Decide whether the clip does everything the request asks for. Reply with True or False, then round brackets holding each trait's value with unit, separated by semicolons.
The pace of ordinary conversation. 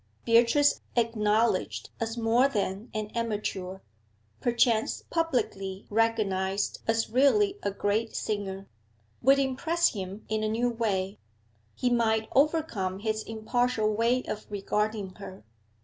False (115 wpm)